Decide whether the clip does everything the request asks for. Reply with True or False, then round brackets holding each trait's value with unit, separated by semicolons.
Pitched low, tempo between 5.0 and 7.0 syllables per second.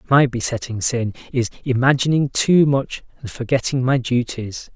False (125 Hz; 4.7 syllables/s)